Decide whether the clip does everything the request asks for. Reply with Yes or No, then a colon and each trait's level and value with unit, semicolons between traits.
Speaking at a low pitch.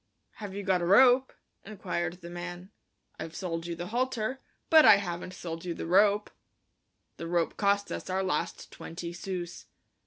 No: medium, 185 Hz